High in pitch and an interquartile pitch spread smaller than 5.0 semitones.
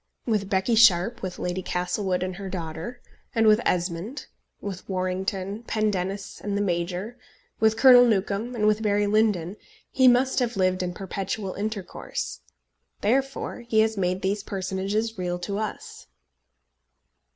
Yes: high, 200 Hz; average, 3.0 semitones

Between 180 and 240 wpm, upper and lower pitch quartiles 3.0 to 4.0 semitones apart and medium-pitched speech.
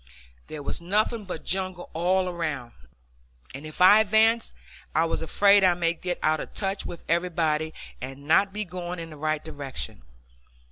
No: average, 170 wpm; average, 3.6 semitones; medium, 175 Hz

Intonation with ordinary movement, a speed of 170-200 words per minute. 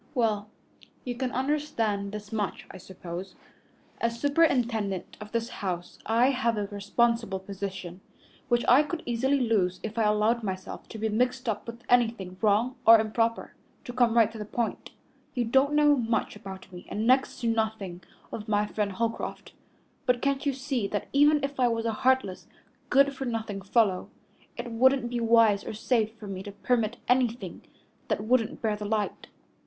Yes: average, 3.2 semitones; average, 175 wpm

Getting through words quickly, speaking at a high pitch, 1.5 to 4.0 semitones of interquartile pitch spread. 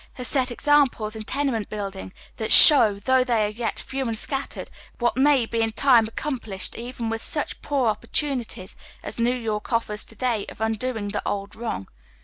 No: average, 185 wpm; high, 230 Hz; average, 3.3 semitones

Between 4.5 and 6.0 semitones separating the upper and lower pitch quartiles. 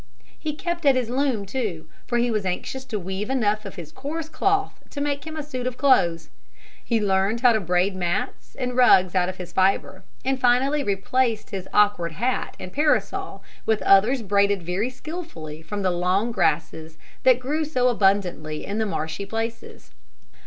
Yes: wide, 5.6 semitones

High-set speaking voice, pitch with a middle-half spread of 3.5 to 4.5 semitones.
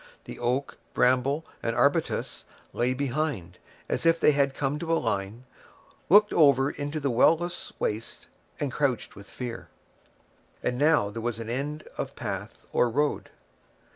No: low, 135 Hz; average, 3.9 semitones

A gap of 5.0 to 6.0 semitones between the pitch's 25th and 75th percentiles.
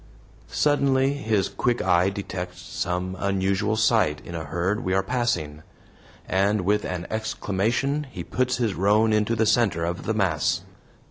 No: average, 3.9 semitones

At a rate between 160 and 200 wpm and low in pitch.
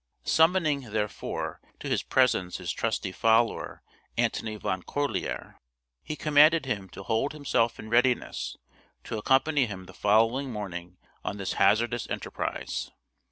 No: slow, 135 wpm; low, 115 Hz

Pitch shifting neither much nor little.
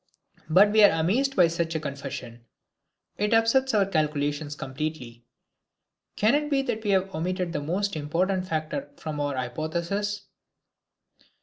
No: wide, 5.7 semitones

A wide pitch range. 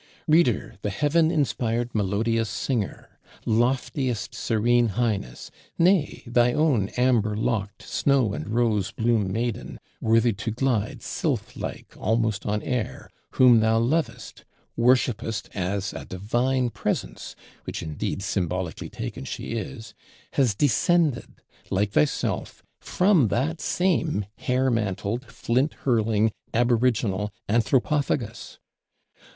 No: average, 3.6 semitones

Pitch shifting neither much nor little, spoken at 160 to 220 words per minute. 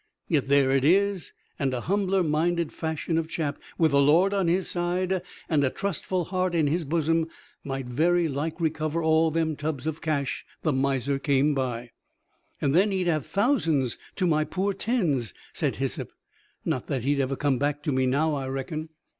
Yes: average, 3.8 semitones; average, 185 wpm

